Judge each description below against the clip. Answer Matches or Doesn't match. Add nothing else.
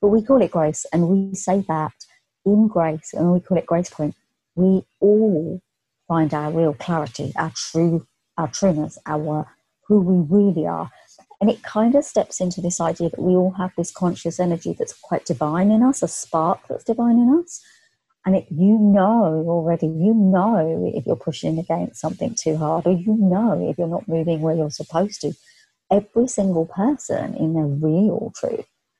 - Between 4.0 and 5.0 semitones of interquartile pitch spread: Matches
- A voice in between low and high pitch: Matches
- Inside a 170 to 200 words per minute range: Matches